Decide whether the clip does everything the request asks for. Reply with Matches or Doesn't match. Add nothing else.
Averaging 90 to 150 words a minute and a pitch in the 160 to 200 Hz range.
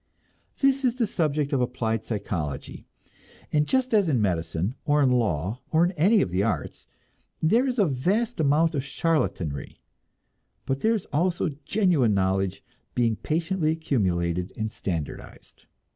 Doesn't match